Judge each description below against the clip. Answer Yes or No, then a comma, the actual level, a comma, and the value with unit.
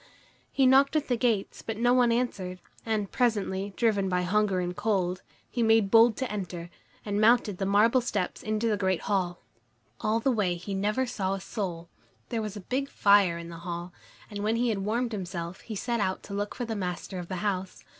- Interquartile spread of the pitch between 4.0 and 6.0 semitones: No, average, 3.6 semitones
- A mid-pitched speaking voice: No, high, 205 Hz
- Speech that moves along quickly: Yes, fast, 210 wpm